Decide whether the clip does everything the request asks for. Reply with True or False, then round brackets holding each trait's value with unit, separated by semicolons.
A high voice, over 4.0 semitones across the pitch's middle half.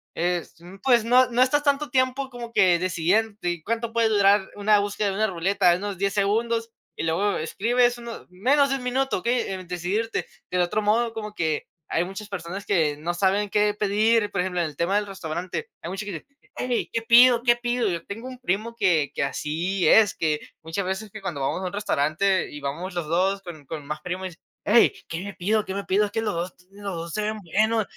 True (200 Hz; 4.4 semitones)